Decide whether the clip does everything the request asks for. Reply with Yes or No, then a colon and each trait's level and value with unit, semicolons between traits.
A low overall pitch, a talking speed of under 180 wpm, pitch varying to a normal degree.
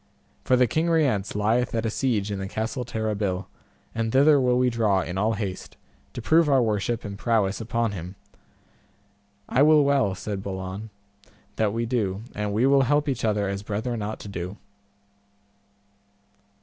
Yes: low, 110 Hz; average, 170 wpm; average, 3.7 semitones